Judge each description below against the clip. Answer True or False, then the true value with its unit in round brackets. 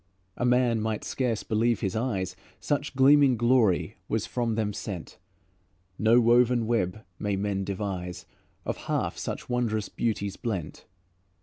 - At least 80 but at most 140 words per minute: True (135 wpm)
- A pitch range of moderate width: True (3.5 semitones)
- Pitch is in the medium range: False (110 Hz)